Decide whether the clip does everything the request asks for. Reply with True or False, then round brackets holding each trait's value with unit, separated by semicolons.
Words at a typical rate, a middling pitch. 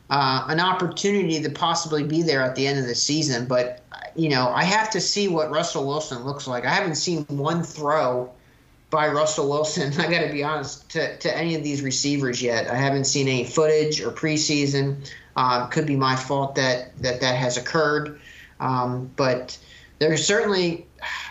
True (185 wpm; 145 Hz)